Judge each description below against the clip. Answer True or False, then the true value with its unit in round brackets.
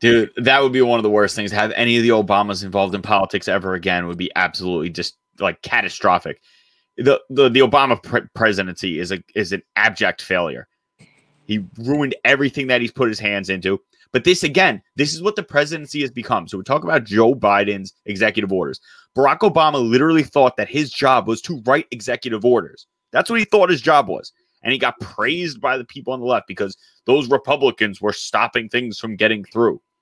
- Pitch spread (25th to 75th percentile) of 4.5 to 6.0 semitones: True (5.5 semitones)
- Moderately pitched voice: False (120 Hz)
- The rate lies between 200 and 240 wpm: True (205 wpm)